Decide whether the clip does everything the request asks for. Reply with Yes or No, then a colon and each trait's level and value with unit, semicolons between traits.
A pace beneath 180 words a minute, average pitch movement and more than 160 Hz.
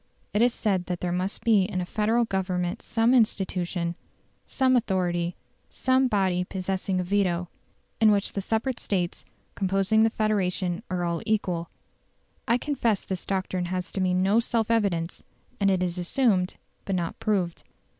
Yes: average, 160 wpm; average, 3.3 semitones; high, 190 Hz